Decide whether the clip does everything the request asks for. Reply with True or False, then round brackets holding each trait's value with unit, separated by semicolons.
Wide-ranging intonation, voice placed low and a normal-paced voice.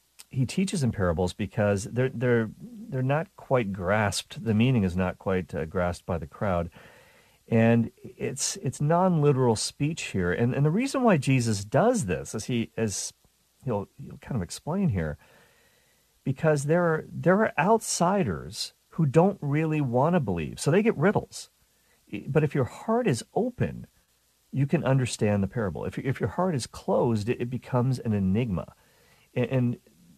True (6.4 semitones; 125 Hz; 165 wpm)